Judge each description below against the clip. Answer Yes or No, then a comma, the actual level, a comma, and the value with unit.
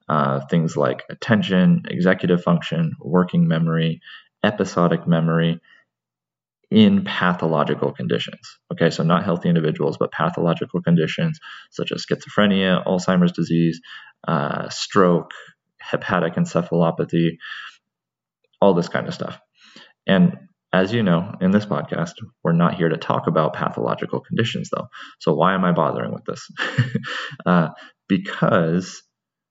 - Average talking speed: No, slow, 120 wpm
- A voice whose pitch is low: Yes, very low, 90 Hz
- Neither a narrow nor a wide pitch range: No, wide, 6.6 semitones